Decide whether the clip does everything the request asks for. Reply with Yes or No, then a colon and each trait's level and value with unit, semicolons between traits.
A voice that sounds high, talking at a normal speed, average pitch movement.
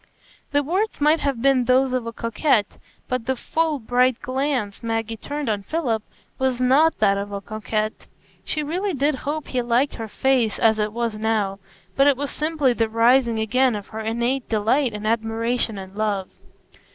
Yes: high, 240 Hz; average, 180 wpm; average, 3.9 semitones